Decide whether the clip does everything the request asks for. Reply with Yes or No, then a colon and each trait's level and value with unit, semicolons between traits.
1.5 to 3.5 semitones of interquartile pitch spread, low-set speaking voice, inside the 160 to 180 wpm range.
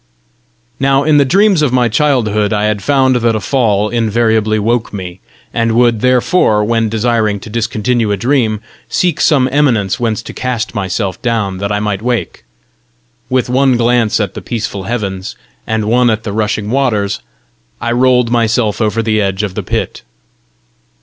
Yes: average, 3.0 semitones; low, 115 Hz; average, 170 wpm